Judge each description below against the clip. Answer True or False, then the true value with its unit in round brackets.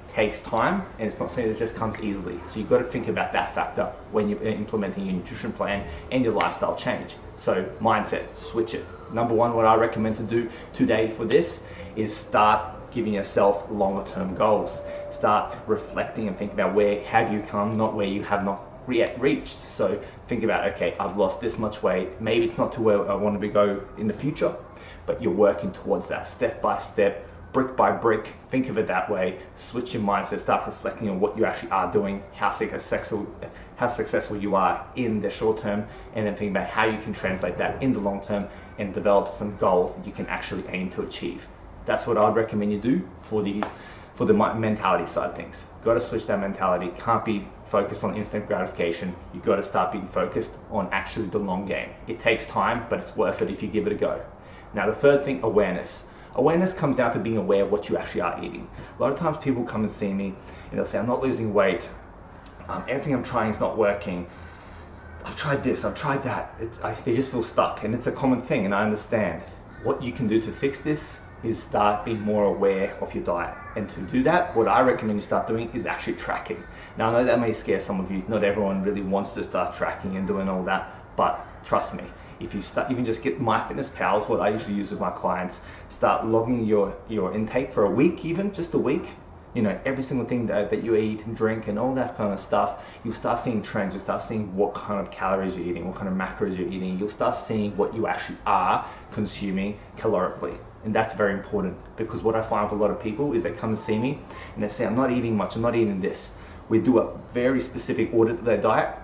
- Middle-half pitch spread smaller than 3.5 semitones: True (2.4 semitones)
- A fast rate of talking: True (230 wpm)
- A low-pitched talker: True (105 Hz)